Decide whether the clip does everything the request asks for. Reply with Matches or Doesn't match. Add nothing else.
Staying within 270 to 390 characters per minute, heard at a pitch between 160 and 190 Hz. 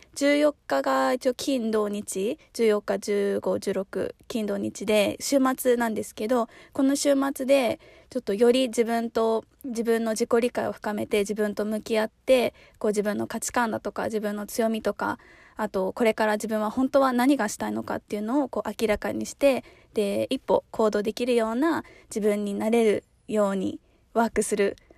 Doesn't match